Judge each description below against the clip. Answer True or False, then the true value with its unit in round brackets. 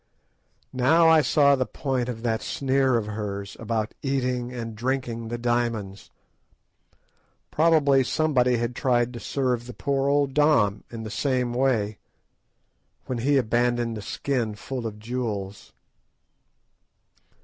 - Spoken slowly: True (130 wpm)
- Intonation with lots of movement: False (3.1 semitones)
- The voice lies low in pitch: True (125 Hz)